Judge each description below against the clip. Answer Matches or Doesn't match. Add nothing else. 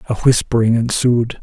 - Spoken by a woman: Doesn't match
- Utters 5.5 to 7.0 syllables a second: Doesn't match